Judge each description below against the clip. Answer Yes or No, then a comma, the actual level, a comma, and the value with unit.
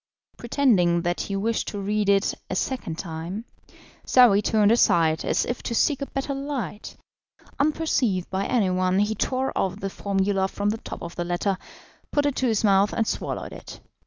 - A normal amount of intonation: Yes, average, 4.4 semitones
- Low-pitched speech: No, high, 205 Hz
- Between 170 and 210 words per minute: Yes, average, 180 wpm